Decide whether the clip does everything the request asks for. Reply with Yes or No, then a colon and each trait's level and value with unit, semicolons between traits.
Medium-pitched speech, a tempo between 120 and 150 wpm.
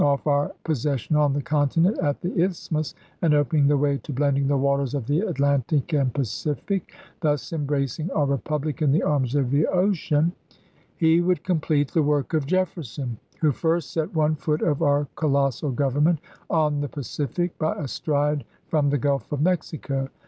No: medium, 145 Hz; average, 180 wpm